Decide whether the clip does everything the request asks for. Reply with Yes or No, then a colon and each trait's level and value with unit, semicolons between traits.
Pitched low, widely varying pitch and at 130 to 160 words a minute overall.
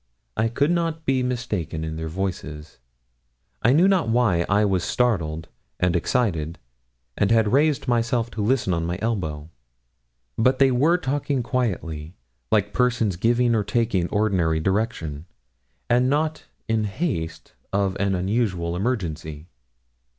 Yes: low, 105 Hz; wide, 6.4 semitones; average, 145 wpm